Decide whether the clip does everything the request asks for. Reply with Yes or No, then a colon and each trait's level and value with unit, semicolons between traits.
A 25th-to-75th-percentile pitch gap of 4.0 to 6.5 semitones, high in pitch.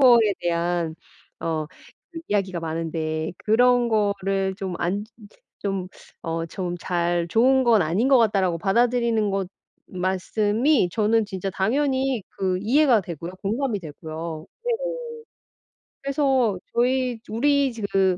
Yes: wide, 5.4 semitones; high, 200 Hz